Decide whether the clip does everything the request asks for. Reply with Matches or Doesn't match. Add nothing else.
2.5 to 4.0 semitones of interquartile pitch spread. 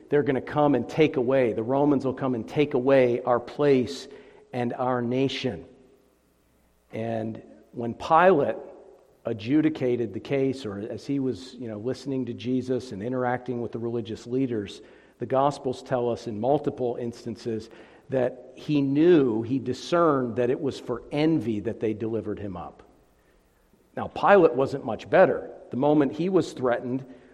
Matches